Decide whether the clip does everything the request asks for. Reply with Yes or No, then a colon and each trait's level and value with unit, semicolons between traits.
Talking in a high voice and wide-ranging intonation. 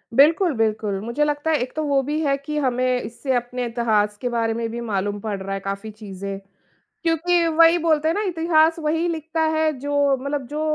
Yes: very high, 275 Hz; wide, 5.8 semitones